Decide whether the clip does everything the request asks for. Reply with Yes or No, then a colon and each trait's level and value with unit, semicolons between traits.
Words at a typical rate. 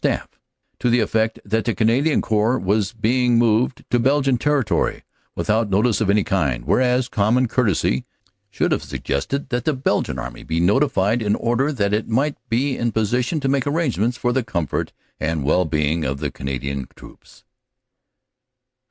Yes: average, 170 wpm